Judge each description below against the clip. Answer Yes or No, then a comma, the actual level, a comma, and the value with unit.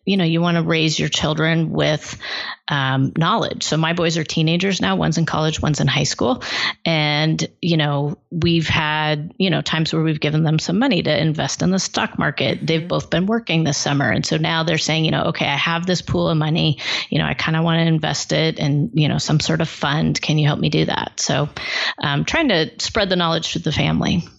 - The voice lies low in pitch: No, medium, 160 Hz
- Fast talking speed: Yes, fast, 235 wpm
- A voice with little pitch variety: Yes, narrow, 1.6 semitones